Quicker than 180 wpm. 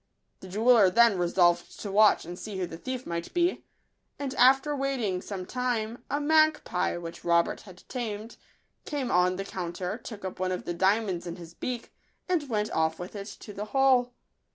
Yes: average, 190 wpm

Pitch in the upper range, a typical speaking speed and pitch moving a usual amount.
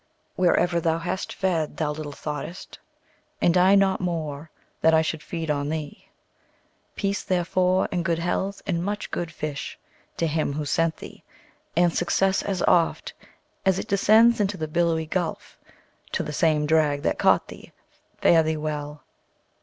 No: medium, 165 Hz; average, 160 wpm; average, 3.0 semitones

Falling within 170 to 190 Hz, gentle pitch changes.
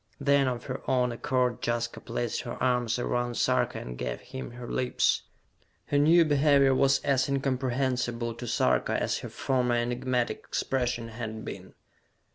No: low, 125 Hz; narrow, 2.0 semitones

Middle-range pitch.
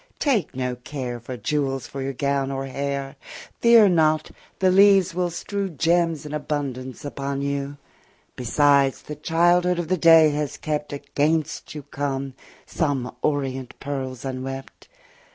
Yes: medium, 145 Hz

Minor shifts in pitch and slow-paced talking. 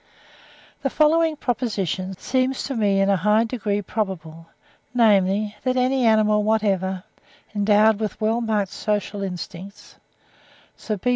No: average, 3.1 semitones; slow, 130 wpm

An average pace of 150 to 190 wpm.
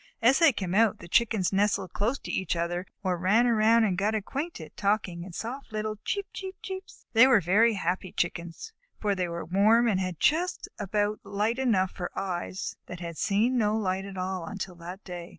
No: fast, 205 wpm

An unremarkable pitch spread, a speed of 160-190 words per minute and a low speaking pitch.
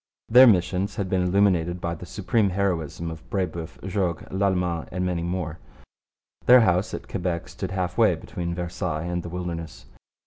No: narrow, 2.1 semitones; average, 165 wpm; very low, 90 Hz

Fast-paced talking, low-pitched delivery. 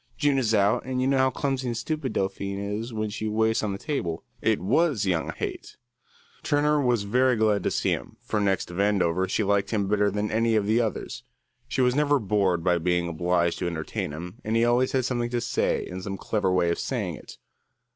Yes: fast, 220 wpm; low, 105 Hz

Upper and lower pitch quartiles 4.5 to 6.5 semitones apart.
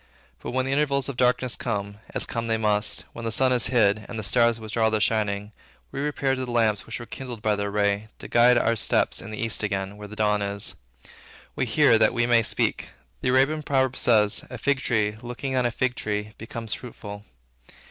No: average, 3.1 semitones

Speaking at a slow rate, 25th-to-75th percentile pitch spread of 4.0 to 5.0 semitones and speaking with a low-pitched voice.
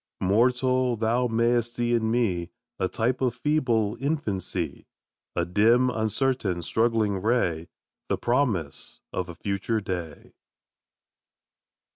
Yes: slow, 110 wpm; average, 4.6 semitones; low, 115 Hz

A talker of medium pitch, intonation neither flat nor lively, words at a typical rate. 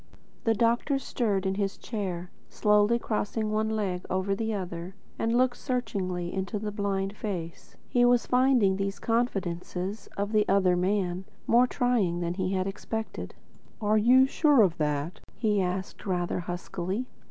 No: high, 200 Hz; average, 3.6 semitones; average, 155 wpm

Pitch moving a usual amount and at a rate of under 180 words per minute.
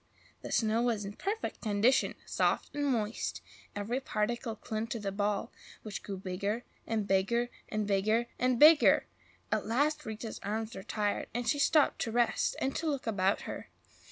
Yes: average, 3.0 semitones; average, 170 wpm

